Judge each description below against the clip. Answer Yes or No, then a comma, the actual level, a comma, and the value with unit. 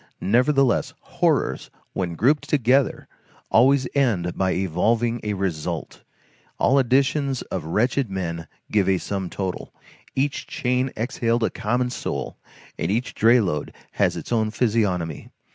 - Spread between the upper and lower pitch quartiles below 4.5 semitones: No, average, 5.2 semitones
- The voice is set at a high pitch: No, low, 115 Hz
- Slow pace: Yes, slow, 130 wpm